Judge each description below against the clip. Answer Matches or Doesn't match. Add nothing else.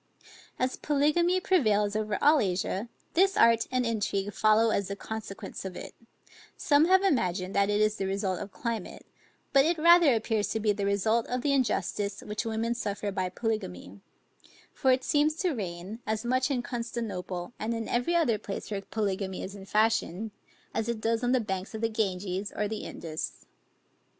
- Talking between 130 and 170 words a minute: Doesn't match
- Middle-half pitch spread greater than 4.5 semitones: Doesn't match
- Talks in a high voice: Matches